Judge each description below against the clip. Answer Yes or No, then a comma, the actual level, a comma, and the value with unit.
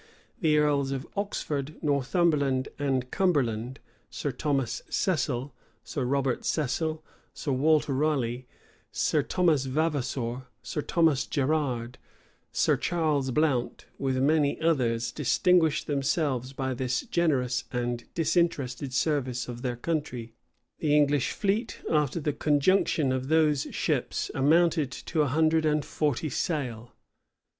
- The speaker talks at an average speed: No, slow, 120 wpm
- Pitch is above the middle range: No, medium, 140 Hz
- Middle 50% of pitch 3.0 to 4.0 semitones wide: Yes, average, 3.4 semitones